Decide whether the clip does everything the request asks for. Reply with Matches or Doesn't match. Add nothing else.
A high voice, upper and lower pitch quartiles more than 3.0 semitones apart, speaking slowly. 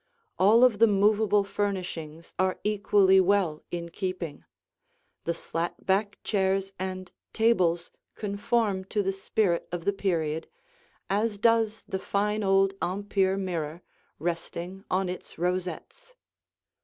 Doesn't match